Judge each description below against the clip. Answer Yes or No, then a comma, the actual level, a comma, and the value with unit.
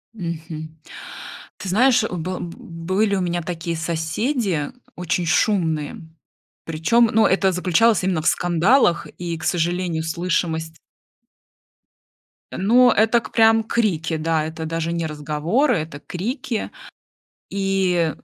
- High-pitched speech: No, medium, 175 Hz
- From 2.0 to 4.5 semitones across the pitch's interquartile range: Yes, average, 4.1 semitones